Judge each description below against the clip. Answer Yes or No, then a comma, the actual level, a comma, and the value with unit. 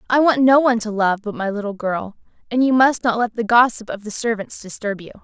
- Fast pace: Yes, fast, 250 wpm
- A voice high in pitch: Yes, high, 225 Hz